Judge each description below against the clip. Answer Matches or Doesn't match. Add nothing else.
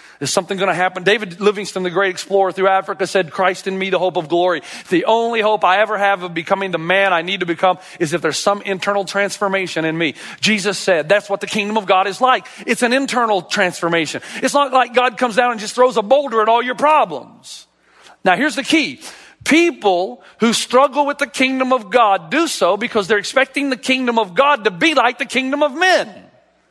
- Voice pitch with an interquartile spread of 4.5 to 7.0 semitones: Matches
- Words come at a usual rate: Doesn't match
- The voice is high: Matches